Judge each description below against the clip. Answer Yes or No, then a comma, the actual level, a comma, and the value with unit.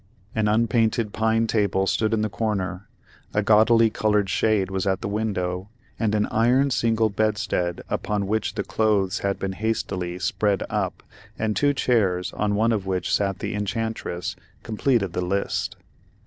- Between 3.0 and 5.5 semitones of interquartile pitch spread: No, narrow, 2.4 semitones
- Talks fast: No, average, 160 wpm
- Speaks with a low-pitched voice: Yes, low, 105 Hz